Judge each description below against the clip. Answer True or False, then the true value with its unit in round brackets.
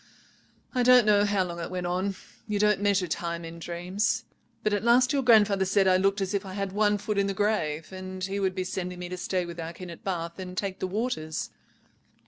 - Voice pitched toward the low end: False (190 Hz)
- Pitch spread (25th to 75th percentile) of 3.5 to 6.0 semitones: False (2.5 semitones)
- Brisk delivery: True (225 wpm)